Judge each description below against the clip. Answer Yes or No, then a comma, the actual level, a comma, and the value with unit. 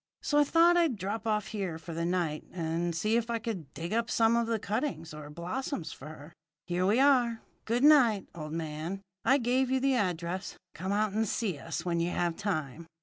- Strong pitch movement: Yes, wide, 5.8 semitones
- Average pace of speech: No, fast, 210 wpm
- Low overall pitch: No, high, 195 Hz